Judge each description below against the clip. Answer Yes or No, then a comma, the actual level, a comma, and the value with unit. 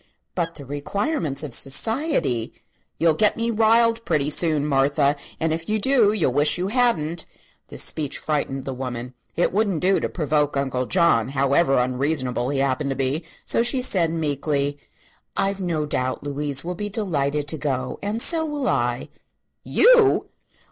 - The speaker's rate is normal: Yes, average, 165 wpm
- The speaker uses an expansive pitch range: Yes, wide, 6.7 semitones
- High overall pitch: No, medium, 155 Hz